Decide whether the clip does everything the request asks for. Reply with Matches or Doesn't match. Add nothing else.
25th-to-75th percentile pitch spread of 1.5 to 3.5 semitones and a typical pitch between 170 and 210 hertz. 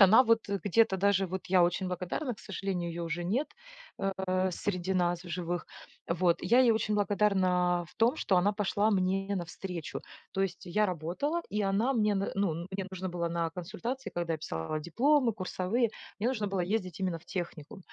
Matches